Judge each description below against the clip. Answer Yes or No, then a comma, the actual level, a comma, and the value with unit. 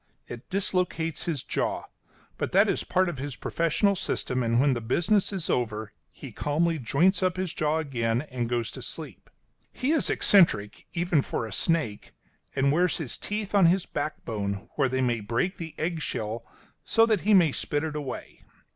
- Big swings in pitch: Yes, wide, 6.8 semitones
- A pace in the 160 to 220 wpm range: Yes, average, 185 wpm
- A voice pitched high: No, medium, 150 Hz